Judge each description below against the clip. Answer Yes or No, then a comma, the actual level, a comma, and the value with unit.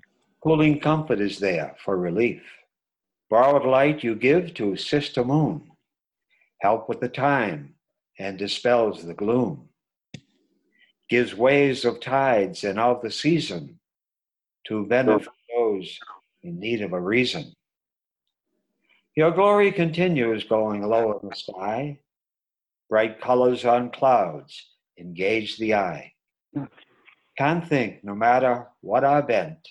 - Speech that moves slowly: Yes, slow, 120 wpm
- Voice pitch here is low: Yes, low, 125 Hz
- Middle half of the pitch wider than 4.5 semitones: Yes, average, 5.0 semitones